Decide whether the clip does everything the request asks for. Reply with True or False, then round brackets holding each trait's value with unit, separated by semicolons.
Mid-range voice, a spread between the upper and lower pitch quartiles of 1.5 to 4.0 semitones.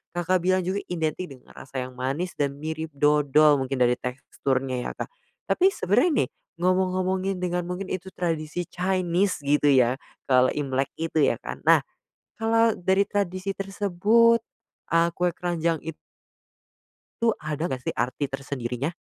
False (165 Hz; 5.1 semitones)